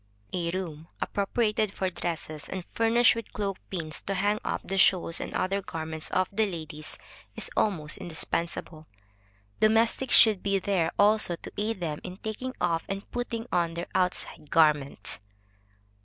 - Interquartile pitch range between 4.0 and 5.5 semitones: Yes, average, 4.3 semitones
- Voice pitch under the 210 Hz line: Yes, medium, 185 Hz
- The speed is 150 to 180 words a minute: Yes, average, 155 wpm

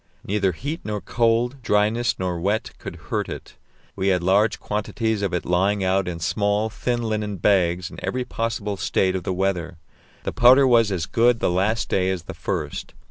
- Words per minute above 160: Yes, average, 190 wpm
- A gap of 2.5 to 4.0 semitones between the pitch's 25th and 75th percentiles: Yes, average, 3.5 semitones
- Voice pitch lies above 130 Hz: No, low, 100 Hz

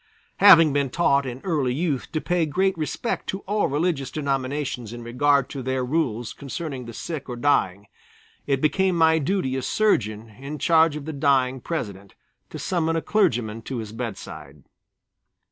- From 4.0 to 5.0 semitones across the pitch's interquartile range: Yes, average, 4.7 semitones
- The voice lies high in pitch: No, medium, 140 Hz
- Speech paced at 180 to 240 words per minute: No, average, 165 wpm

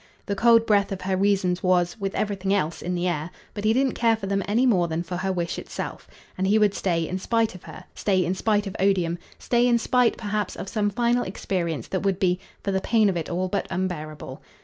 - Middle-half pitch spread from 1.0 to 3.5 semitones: Yes, average, 3.0 semitones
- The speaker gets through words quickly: Yes, fast, 240 wpm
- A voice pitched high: Yes, high, 195 Hz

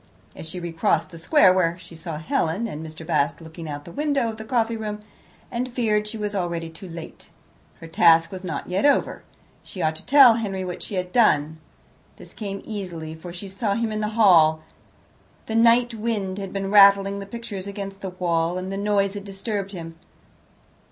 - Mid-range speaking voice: No, high, 195 Hz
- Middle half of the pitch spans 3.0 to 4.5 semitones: Yes, average, 4.2 semitones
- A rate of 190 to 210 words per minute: Yes, average, 200 wpm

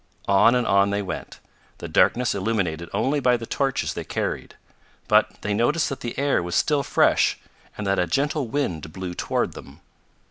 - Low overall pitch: Yes, low, 115 Hz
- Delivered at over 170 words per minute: Yes, average, 180 wpm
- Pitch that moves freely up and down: Yes, wide, 6.6 semitones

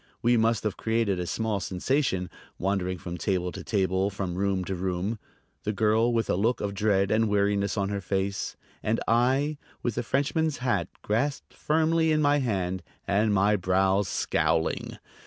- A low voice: Yes, low, 105 Hz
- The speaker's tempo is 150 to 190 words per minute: Yes, average, 170 wpm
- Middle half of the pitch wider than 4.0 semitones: No, average, 3.5 semitones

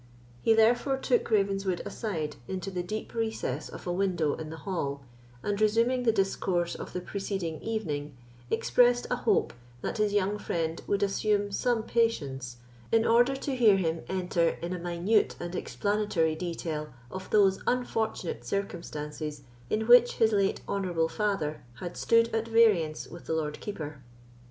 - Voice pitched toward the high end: Yes, high, 195 Hz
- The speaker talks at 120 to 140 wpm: No, average, 155 wpm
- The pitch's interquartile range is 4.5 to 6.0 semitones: Yes, average, 5.1 semitones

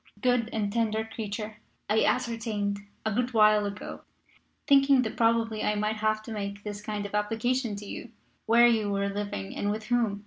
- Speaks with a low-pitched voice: No, high, 215 Hz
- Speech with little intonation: Yes, narrow, 2.0 semitones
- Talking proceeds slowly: No, average, 180 wpm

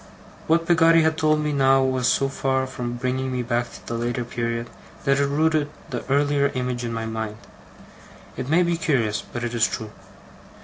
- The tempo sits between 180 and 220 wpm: Yes, average, 190 wpm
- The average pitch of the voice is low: Yes, low, 130 Hz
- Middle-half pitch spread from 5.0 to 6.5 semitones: No, average, 3.5 semitones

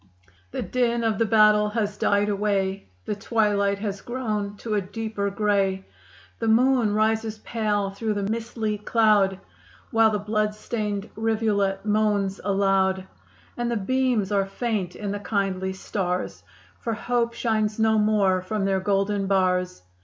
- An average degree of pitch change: No, narrow, 2.1 semitones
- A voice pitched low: No, high, 210 Hz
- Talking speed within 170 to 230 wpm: No, average, 145 wpm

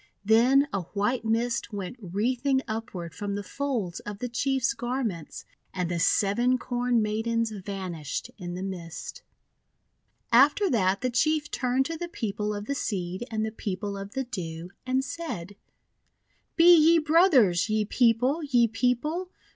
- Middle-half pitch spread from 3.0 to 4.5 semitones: No, average, 4.9 semitones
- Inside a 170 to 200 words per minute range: No, average, 155 wpm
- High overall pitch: Yes, high, 230 Hz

